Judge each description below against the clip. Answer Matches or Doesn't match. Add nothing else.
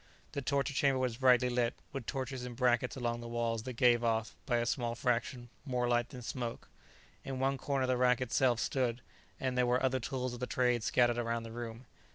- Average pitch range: Doesn't match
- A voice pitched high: Doesn't match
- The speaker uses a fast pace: Matches